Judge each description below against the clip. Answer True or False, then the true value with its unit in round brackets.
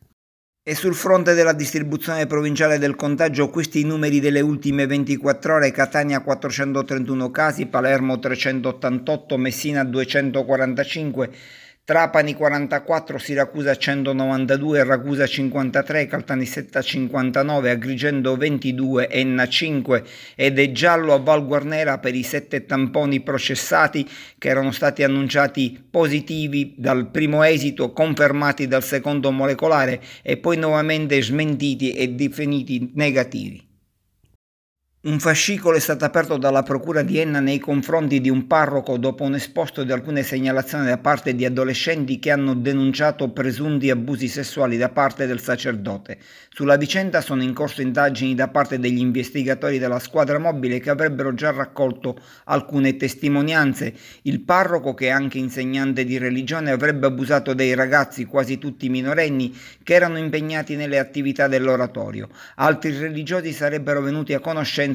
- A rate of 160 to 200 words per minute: False (130 wpm)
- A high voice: False (140 Hz)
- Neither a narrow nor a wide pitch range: False (2.2 semitones)